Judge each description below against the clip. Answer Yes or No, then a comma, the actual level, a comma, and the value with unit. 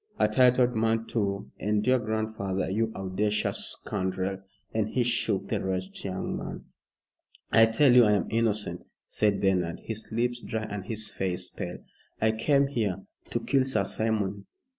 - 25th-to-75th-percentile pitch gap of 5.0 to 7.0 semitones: No, average, 2.7 semitones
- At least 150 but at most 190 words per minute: Yes, average, 160 wpm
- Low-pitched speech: Yes, low, 110 Hz